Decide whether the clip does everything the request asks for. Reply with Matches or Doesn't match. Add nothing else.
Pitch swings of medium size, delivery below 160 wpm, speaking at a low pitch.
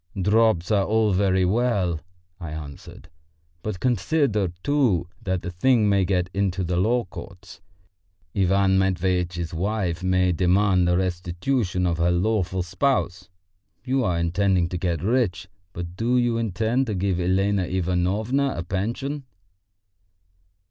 Matches